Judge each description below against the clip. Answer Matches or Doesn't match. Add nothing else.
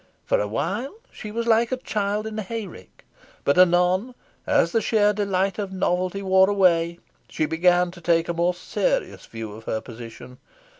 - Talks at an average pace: Matches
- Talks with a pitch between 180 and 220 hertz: Matches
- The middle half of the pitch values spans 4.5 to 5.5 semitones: Doesn't match